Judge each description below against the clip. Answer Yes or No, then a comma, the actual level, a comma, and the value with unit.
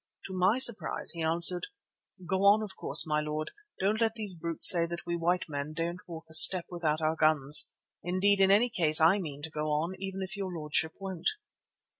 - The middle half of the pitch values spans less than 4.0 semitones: Yes, average, 3.4 semitones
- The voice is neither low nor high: Yes, medium, 170 Hz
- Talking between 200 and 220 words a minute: Yes, fast, 205 wpm